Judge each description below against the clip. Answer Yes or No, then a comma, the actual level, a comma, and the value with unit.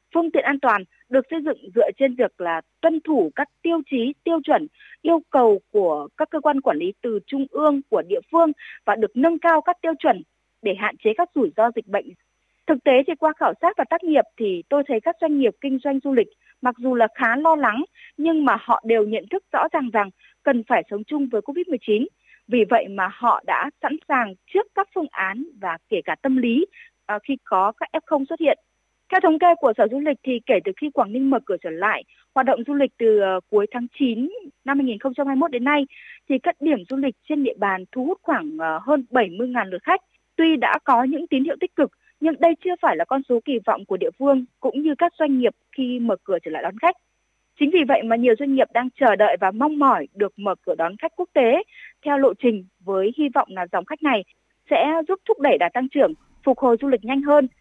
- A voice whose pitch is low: No, very high, 275 Hz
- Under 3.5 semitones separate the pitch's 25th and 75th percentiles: No, wide, 5.6 semitones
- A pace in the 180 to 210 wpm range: No, average, 235 wpm